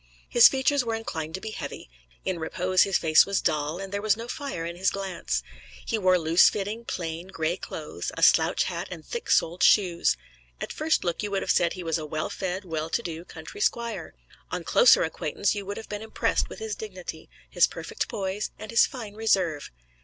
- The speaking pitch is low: No, high, 195 Hz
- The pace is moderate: No, fast, 210 wpm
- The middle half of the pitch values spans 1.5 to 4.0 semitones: No, average, 4.8 semitones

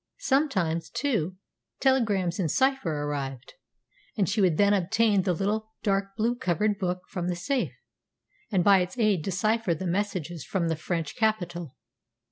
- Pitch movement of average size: Yes, average, 4.0 semitones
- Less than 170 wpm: Yes, average, 150 wpm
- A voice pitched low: No, high, 190 Hz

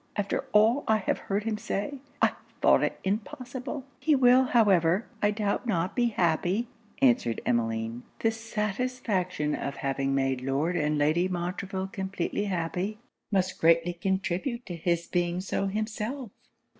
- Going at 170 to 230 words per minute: No, average, 145 wpm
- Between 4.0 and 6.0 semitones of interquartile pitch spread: Yes, average, 4.7 semitones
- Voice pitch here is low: No, high, 195 Hz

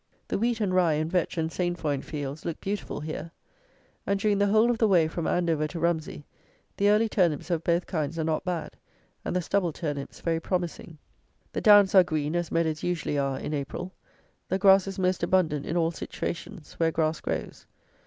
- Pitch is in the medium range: Yes, medium, 170 Hz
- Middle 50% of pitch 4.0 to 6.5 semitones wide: No, average, 3.2 semitones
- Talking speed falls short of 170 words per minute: No, average, 195 wpm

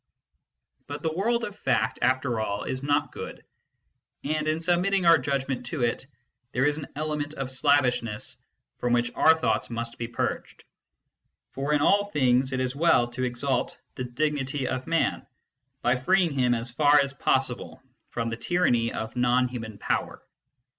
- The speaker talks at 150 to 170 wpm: Yes, average, 165 wpm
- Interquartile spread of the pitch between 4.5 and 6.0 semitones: No, average, 3.7 semitones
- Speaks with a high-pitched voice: No, low, 135 Hz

